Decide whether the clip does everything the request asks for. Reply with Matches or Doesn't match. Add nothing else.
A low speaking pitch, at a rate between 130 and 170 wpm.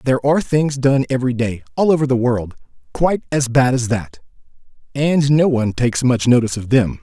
Doesn't match